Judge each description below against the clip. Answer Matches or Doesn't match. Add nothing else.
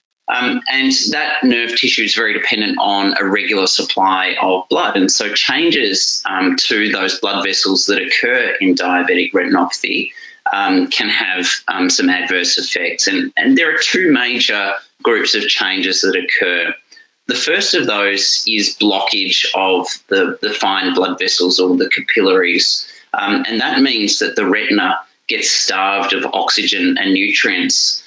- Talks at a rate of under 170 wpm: Matches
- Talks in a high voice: Matches